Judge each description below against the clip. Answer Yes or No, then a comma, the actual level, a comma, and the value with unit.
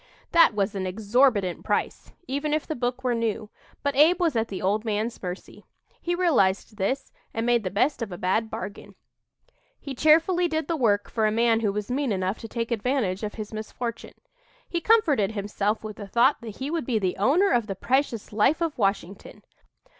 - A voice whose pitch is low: No, high, 230 Hz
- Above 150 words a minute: Yes, average, 200 wpm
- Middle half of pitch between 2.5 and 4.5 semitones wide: No, average, 5.3 semitones